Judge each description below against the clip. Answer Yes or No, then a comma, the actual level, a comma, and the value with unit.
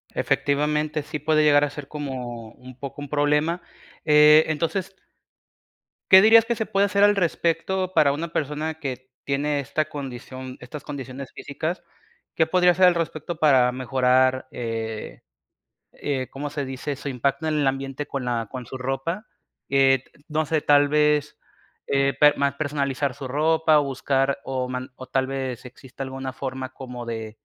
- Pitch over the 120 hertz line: Yes, medium, 140 Hz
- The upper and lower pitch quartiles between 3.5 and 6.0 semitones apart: No, average, 2.9 semitones